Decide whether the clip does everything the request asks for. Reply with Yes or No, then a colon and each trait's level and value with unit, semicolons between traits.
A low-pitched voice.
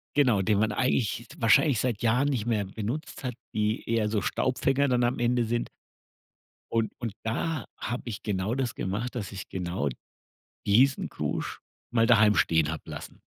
Yes: low, 115 Hz